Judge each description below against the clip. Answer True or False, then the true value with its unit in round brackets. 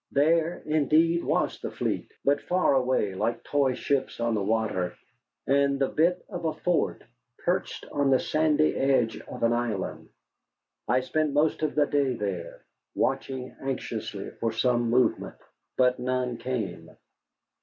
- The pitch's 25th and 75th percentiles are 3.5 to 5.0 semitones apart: True (4.2 semitones)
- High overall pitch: False (130 Hz)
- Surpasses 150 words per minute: False (145 wpm)